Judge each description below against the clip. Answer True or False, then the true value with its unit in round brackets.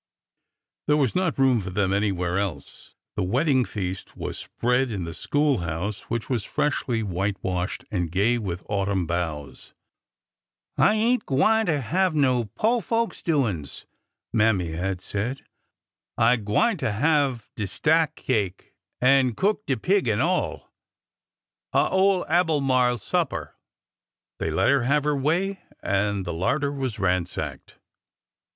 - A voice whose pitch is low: True (120 Hz)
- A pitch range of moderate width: False (7.5 semitones)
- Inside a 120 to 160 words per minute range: True (140 wpm)